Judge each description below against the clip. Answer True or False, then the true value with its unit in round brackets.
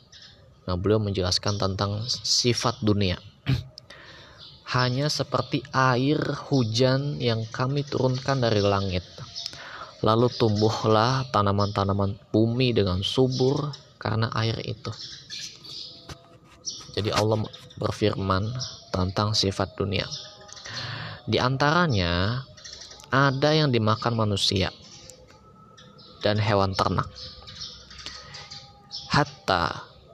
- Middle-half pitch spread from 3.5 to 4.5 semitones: True (4.2 semitones)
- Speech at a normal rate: False (80 wpm)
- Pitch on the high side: False (115 Hz)